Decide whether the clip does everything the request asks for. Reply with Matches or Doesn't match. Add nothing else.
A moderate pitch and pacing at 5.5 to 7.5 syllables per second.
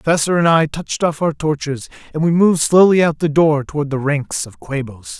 Matches